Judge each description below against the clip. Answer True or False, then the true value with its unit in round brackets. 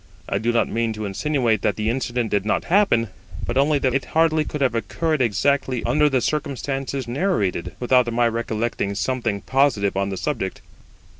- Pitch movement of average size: True (4.1 semitones)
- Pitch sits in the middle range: False (120 Hz)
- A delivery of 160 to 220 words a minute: True (175 wpm)